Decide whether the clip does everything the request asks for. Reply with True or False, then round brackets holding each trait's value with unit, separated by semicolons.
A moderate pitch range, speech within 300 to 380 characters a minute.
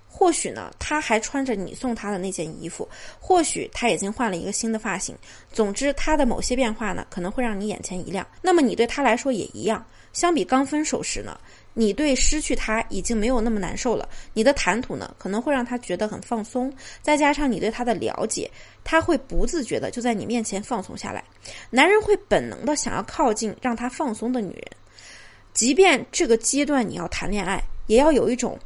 True (4.8 semitones; 310 characters per minute)